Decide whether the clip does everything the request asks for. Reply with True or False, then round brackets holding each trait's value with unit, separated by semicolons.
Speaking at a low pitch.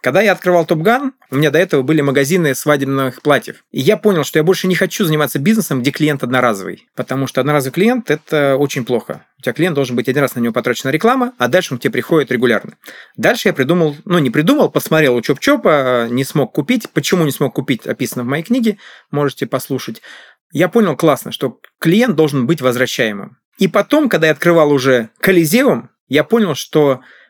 False (150 Hz)